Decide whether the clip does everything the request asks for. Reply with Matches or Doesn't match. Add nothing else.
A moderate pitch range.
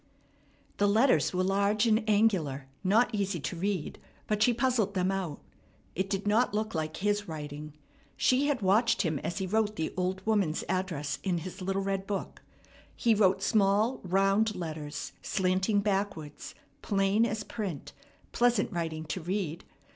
Matches